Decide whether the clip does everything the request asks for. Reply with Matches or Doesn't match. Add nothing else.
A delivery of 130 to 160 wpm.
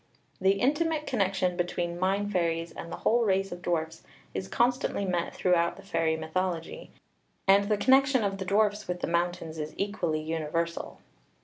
Doesn't match